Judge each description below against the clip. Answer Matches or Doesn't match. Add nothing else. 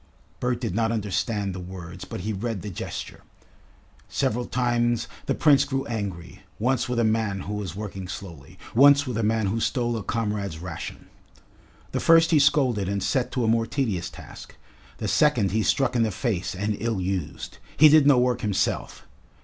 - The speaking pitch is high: Doesn't match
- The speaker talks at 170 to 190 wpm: Matches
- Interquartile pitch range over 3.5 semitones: Matches